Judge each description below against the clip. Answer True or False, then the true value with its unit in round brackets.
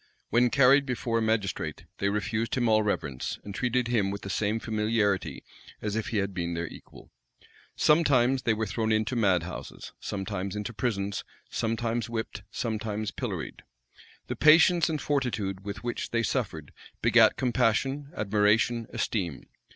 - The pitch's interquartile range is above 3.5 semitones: False (3.2 semitones)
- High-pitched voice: False (110 Hz)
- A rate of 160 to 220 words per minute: False (150 wpm)